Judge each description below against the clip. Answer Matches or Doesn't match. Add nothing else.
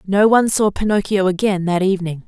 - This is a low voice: Doesn't match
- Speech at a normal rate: Matches